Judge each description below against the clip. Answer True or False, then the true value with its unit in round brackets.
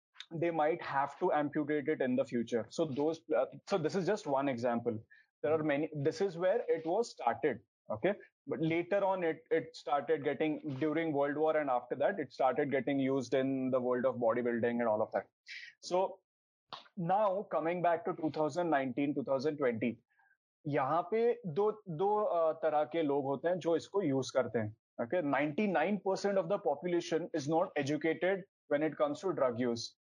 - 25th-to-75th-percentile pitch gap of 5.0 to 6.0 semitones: False (4.4 semitones)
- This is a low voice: False (155 Hz)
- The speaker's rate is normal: True (150 wpm)